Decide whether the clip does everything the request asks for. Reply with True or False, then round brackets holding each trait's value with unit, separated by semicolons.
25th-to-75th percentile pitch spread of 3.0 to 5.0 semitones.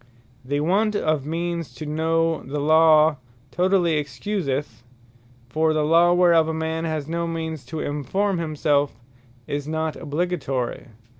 False (2.4 semitones)